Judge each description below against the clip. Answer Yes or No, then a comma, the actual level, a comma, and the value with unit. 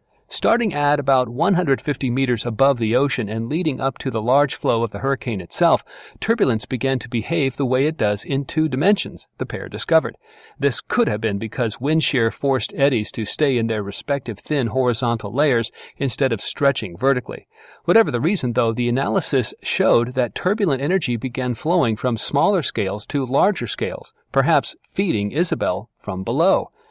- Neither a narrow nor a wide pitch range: Yes, average, 3.5 semitones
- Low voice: Yes, low, 130 Hz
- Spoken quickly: No, average, 170 wpm